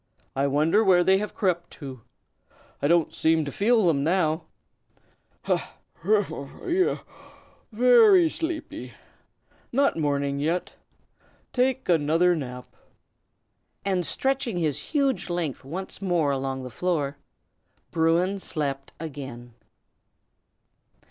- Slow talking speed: Yes, slow, 110 wpm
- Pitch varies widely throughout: Yes, wide, 6.0 semitones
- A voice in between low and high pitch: Yes, medium, 170 Hz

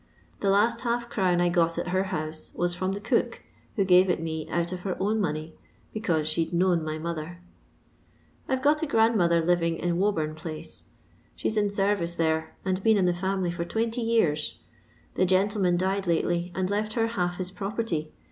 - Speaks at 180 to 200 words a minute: Yes, average, 195 wpm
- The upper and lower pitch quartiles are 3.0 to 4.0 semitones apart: Yes, average, 3.3 semitones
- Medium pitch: Yes, medium, 180 Hz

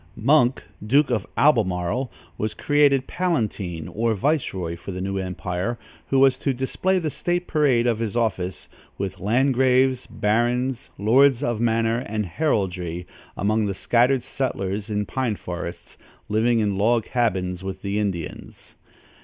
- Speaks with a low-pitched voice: Yes, low, 115 Hz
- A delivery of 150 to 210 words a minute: No, average, 140 wpm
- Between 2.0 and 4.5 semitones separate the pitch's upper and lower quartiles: No, average, 5.1 semitones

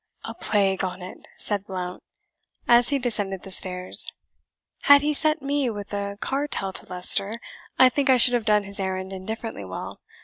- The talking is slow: No, average, 175 wpm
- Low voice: No, high, 205 Hz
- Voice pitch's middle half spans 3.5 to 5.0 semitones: Yes, average, 4.7 semitones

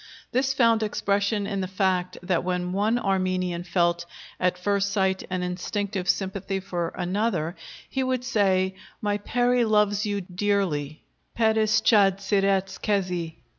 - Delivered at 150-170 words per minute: No, slow, 135 wpm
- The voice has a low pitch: No, high, 195 Hz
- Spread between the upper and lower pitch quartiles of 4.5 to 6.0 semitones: No, narrow, 2.4 semitones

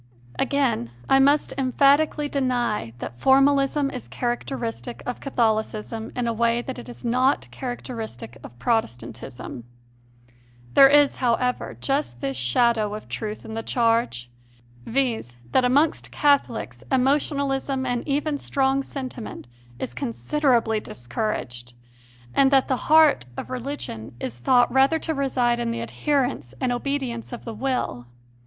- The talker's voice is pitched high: Yes, high, 245 Hz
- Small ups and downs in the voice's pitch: No, average, 3.9 semitones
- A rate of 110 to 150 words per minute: Yes, slow, 135 wpm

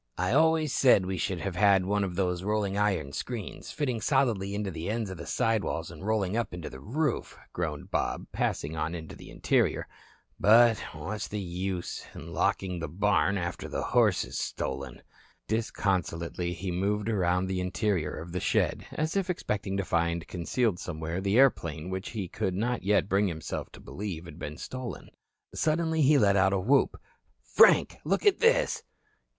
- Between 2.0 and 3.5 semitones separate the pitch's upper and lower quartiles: No, average, 4.1 semitones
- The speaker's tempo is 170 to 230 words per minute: Yes, average, 180 wpm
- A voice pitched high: No, low, 100 Hz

